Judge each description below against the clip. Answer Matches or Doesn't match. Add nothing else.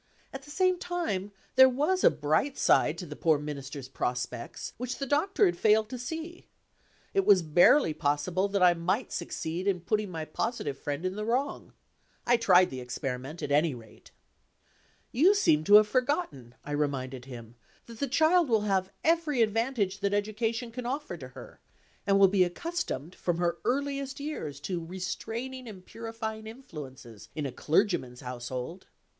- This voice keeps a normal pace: Matches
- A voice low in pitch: Doesn't match